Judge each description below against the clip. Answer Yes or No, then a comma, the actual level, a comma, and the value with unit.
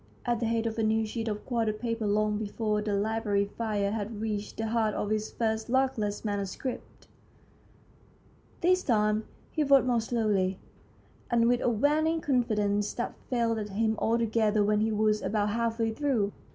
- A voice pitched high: Yes, high, 220 Hz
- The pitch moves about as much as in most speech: No, narrow, 1.8 semitones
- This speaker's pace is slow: No, average, 165 wpm